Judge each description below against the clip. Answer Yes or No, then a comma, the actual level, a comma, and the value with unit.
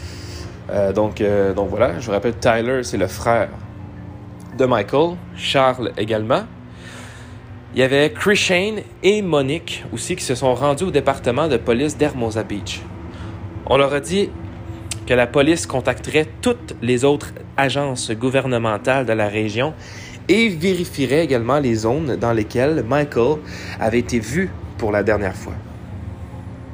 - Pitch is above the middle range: No, low, 115 Hz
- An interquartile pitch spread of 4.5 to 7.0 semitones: Yes, average, 5.1 semitones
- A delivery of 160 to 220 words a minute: No, slow, 145 wpm